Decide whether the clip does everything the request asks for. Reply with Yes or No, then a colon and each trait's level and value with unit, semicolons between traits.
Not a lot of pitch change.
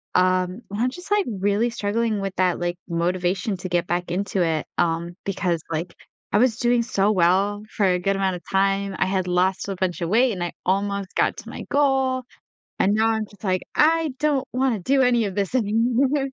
No: average, 4.4 semitones